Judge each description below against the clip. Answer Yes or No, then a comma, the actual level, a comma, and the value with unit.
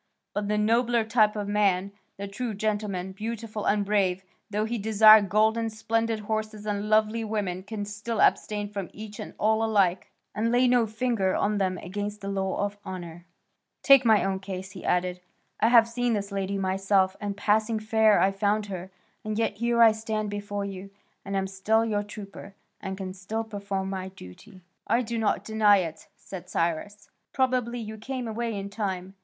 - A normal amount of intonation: No, narrow, 2.1 semitones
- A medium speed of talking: Yes, average, 185 wpm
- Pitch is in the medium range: No, high, 210 Hz